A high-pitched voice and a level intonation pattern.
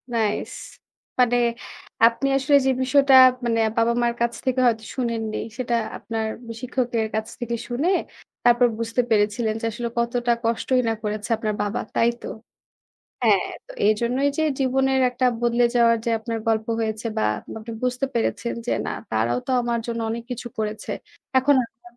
Yes: high, 235 Hz; narrow, 1.8 semitones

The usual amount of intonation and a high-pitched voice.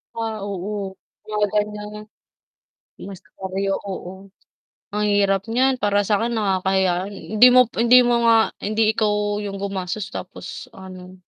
No: narrow, 2.0 semitones; high, 205 Hz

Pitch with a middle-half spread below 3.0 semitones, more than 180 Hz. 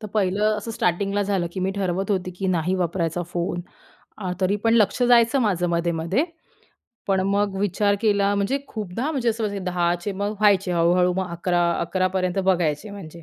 Yes: narrow, 2.6 semitones; high, 190 Hz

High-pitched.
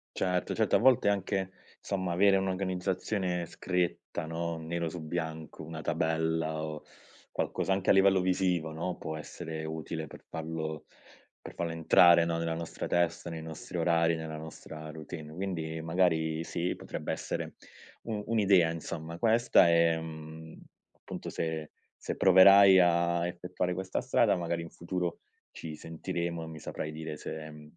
No: very low, 85 Hz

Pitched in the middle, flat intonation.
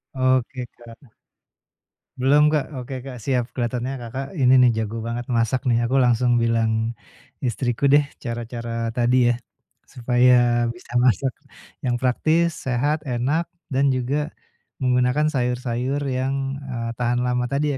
No: low, 125 Hz; narrow, 2.1 semitones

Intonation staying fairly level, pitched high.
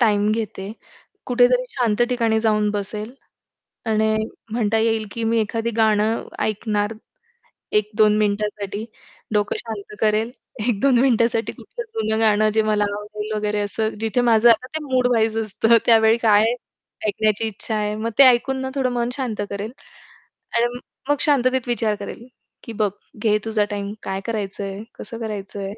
Yes: narrow, 1.9 semitones; high, 220 Hz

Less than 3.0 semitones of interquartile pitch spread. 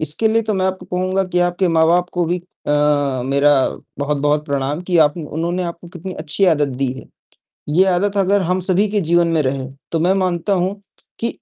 No: average, 3.6 semitones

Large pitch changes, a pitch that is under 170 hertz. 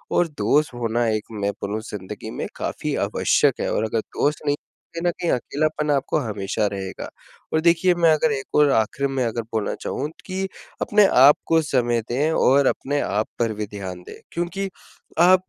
Yes: wide, 6.4 semitones; low, 135 Hz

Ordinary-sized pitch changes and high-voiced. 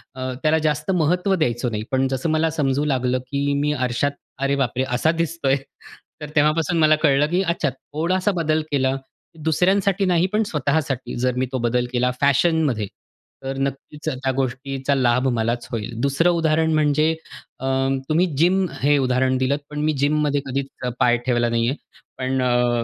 No: average, 3.6 semitones; medium, 140 Hz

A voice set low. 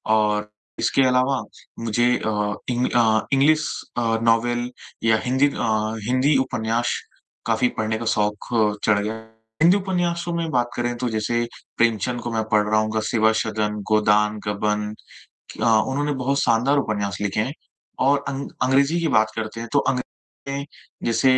Yes: low, 115 Hz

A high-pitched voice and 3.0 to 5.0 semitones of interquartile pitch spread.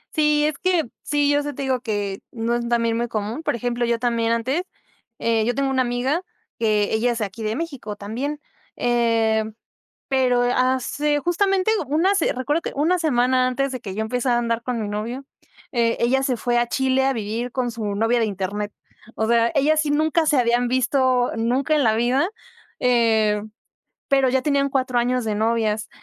Yes: high, 245 Hz; average, 3.3 semitones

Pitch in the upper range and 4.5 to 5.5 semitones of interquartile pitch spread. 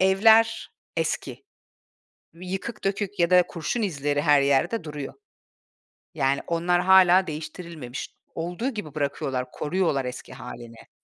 No: medium, 170 Hz; average, 5.0 semitones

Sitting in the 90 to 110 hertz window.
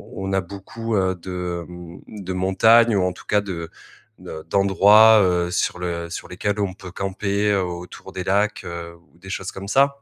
Yes: very low, 95 Hz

